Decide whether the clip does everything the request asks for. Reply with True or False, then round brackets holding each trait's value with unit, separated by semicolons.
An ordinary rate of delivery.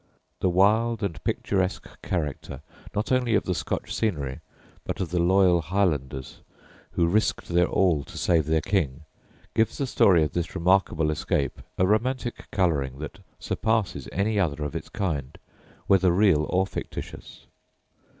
True (150 wpm)